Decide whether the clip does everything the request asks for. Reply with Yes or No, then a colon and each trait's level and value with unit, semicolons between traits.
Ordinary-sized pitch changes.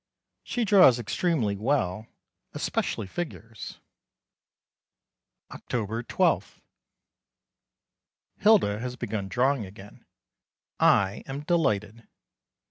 No: wide, 6.0 semitones